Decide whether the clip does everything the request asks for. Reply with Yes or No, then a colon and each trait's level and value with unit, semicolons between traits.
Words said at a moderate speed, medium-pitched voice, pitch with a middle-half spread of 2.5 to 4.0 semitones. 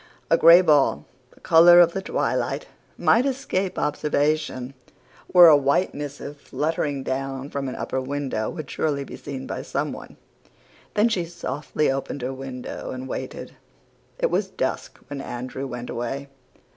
Yes: average, 150 wpm; medium, 145 Hz; average, 3.6 semitones